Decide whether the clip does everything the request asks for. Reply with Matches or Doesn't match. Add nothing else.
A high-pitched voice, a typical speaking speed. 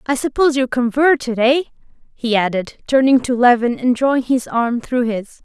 Matches